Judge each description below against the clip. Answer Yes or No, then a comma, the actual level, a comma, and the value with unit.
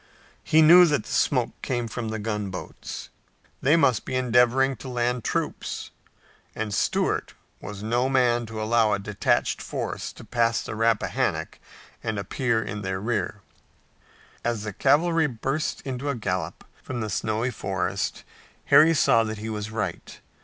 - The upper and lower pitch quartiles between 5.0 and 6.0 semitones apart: No, average, 3.3 semitones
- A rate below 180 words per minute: Yes, average, 150 wpm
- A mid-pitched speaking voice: No, low, 115 Hz